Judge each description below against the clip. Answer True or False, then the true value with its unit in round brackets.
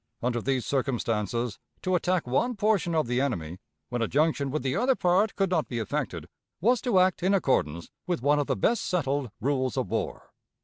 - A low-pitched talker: False (145 Hz)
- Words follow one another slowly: False (195 wpm)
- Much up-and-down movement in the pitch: True (7.0 semitones)